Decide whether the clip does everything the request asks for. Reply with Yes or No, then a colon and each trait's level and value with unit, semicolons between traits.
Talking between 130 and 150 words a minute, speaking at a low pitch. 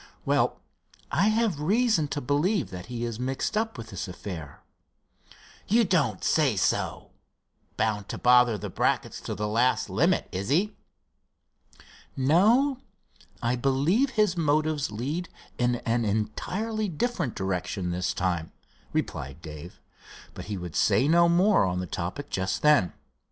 Yes: average, 140 wpm; low, 130 Hz